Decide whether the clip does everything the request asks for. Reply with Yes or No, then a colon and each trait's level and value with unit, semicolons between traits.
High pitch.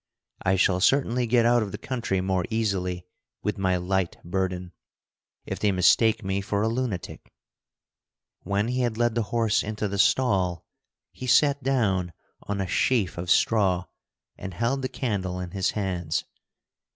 No: low, 100 Hz